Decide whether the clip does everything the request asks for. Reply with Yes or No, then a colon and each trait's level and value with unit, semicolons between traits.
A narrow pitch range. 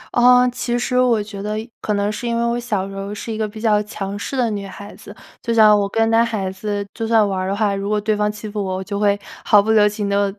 Yes: narrow, 1.9 semitones